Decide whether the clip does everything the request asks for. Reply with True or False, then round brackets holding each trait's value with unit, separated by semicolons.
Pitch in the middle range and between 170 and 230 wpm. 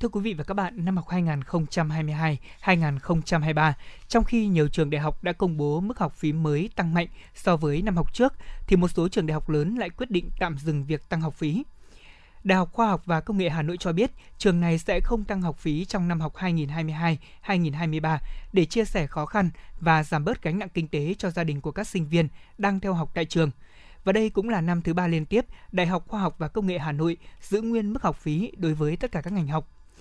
False (170 Hz; 240 wpm)